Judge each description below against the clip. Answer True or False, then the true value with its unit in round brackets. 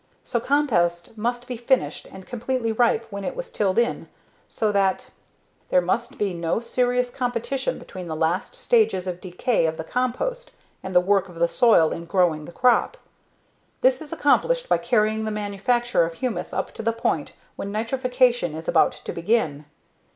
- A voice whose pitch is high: True (220 Hz)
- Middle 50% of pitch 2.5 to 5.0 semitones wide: False (5.5 semitones)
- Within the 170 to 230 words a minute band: True (180 wpm)